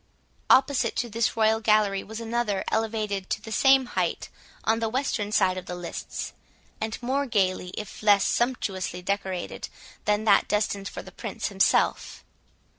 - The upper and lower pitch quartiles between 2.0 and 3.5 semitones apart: Yes, narrow, 2.6 semitones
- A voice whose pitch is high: Yes, high, 215 Hz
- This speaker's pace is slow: No, average, 155 wpm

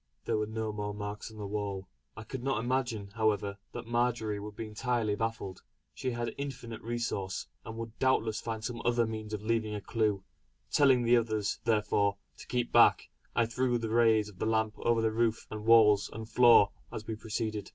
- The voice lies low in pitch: Yes, low, 110 Hz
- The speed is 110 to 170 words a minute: No, average, 195 wpm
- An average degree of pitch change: No, narrow, 1.9 semitones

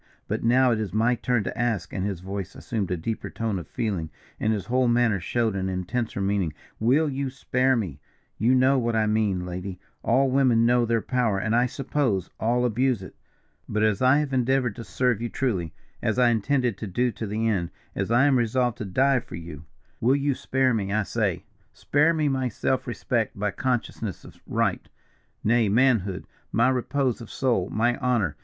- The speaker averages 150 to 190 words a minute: No, average, 200 wpm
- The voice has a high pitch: No, low, 115 Hz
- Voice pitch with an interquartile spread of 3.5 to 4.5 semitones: Yes, average, 4.0 semitones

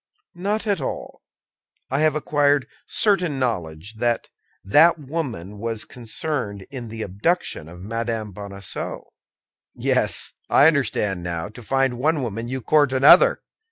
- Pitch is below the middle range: Yes, low, 120 Hz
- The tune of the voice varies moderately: No, wide, 6.1 semitones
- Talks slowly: Yes, slow, 130 wpm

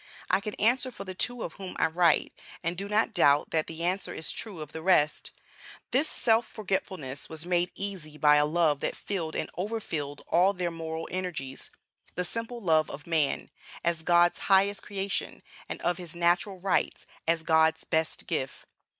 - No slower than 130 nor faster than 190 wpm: Yes, average, 180 wpm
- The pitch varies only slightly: No, average, 3.6 semitones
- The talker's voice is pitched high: No, medium, 175 Hz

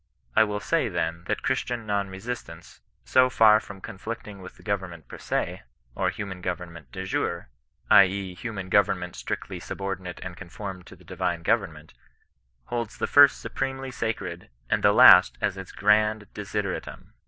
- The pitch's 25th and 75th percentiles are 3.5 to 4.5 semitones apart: No, average, 3.0 semitones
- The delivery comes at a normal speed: Yes, average, 165 wpm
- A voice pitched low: Yes, low, 100 Hz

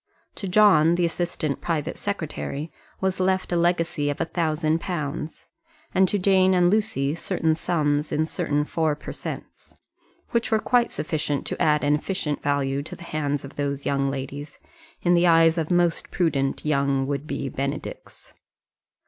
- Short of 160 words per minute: No, average, 165 wpm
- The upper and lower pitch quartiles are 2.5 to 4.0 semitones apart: Yes, average, 3.4 semitones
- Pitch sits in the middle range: Yes, medium, 155 Hz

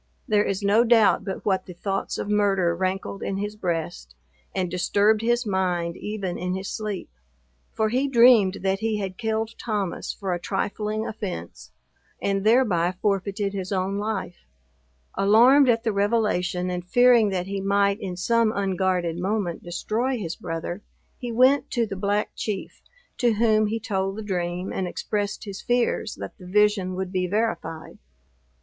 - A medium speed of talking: Yes, average, 165 wpm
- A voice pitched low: No, high, 200 Hz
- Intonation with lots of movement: No, average, 2.8 semitones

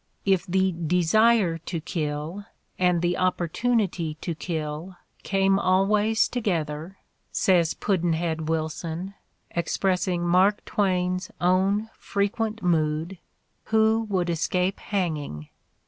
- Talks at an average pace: No, slow, 105 wpm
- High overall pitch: No, medium, 180 Hz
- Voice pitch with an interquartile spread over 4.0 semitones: No, average, 3.0 semitones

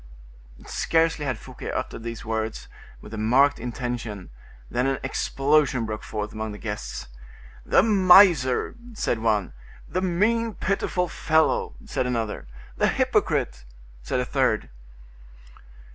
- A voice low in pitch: Yes, low, 125 Hz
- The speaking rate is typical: No, slow, 125 wpm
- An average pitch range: No, wide, 6.7 semitones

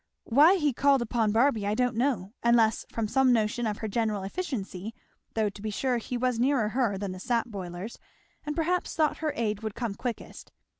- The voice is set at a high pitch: Yes, high, 230 Hz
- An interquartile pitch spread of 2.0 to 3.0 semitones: No, average, 3.6 semitones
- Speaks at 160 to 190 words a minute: No, average, 200 wpm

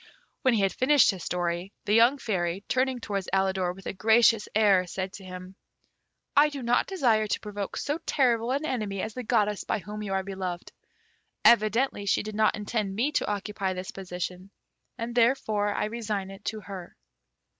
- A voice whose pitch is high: Yes, high, 210 Hz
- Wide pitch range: No, average, 3.5 semitones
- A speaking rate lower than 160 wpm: No, average, 185 wpm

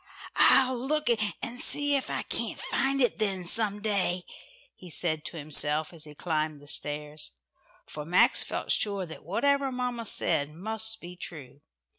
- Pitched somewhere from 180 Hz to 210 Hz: Yes, medium, 185 Hz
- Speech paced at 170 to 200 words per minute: No, average, 160 wpm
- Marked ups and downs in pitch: Yes, wide, 7.8 semitones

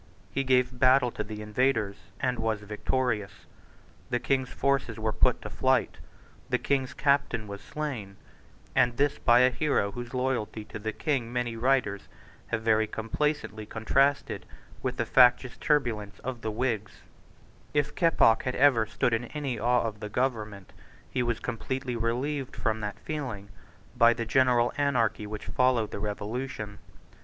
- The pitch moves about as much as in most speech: Yes, average, 3.4 semitones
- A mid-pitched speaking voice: No, low, 120 Hz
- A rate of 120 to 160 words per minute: Yes, average, 155 wpm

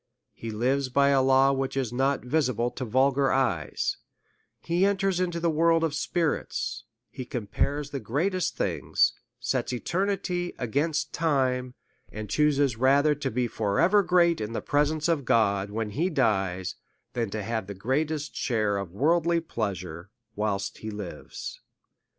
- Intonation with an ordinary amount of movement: No, wide, 6.1 semitones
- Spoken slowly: No, average, 155 wpm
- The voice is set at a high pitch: No, low, 135 Hz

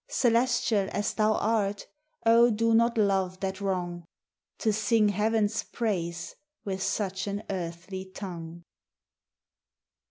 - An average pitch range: Yes, average, 3.0 semitones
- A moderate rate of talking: No, slow, 115 wpm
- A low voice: No, high, 200 Hz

